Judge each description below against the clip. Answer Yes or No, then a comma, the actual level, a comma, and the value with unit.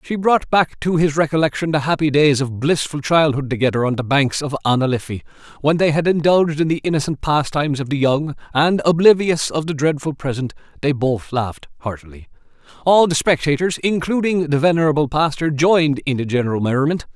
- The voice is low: No, medium, 150 Hz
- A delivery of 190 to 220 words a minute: No, average, 180 wpm